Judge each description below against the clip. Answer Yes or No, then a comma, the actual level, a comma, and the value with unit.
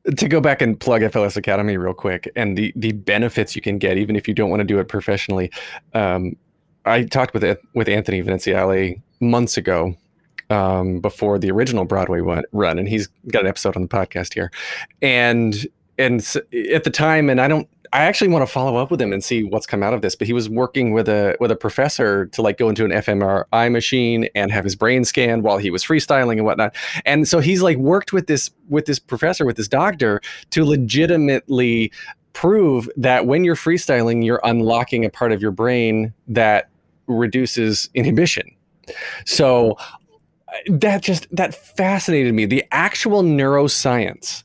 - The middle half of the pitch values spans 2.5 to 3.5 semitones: No, average, 4.7 semitones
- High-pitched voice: No, low, 115 Hz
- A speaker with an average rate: Yes, average, 190 wpm